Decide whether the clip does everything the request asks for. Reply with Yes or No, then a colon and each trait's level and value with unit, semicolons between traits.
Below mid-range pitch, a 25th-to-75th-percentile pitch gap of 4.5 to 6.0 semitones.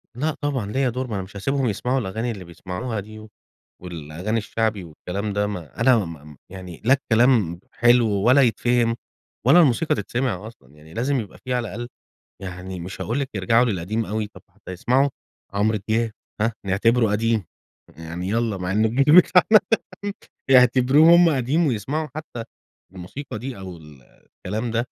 Yes: low, 110 Hz; average, 5.0 semitones